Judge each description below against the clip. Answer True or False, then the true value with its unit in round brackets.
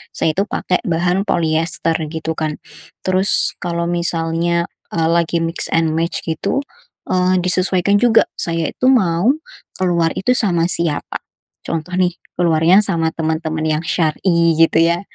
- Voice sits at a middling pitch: True (170 Hz)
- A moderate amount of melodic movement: False (1.9 semitones)